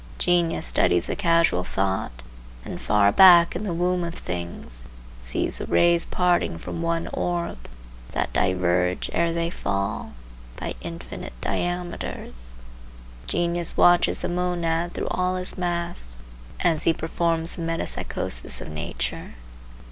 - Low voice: No, medium, 165 Hz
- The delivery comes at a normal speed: No, slow, 130 wpm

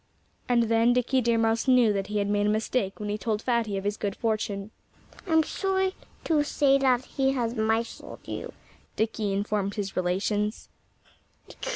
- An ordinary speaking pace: Yes, average, 170 wpm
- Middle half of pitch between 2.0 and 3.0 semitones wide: No, average, 3.4 semitones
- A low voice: No, high, 225 Hz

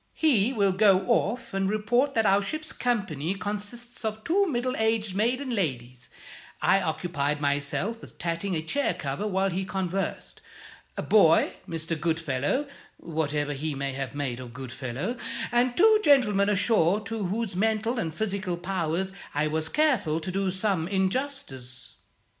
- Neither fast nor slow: Yes, average, 150 wpm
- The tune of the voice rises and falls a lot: Yes, wide, 5.9 semitones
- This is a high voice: Yes, high, 195 Hz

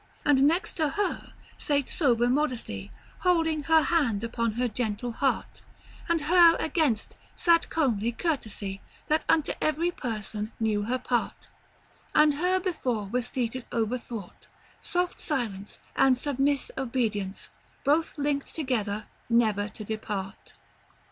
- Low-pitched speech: No, very high, 255 Hz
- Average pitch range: No, wide, 5.8 semitones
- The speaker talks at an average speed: No, slow, 125 wpm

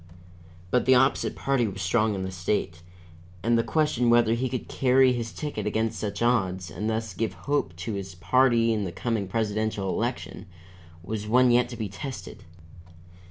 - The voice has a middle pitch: No, low, 110 Hz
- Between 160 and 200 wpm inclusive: Yes, average, 175 wpm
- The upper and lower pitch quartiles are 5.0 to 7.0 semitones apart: No, average, 3.8 semitones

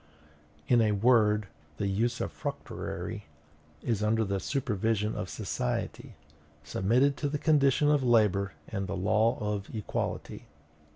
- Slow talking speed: Yes, slow, 120 wpm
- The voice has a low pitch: Yes, low, 110 Hz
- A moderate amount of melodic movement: Yes, average, 3.6 semitones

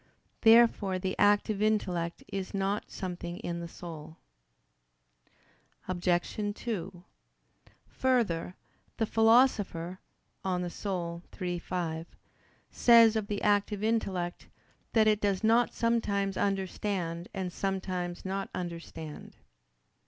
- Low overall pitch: No, high, 195 Hz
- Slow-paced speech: Yes, slow, 100 wpm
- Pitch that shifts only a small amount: No, average, 3.3 semitones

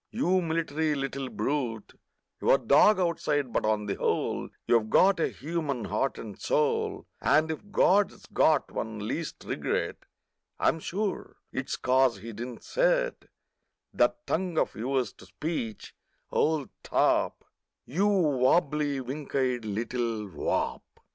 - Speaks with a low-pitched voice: No, medium, 145 Hz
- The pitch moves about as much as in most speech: No, wide, 6.6 semitones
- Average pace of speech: No, slow, 130 wpm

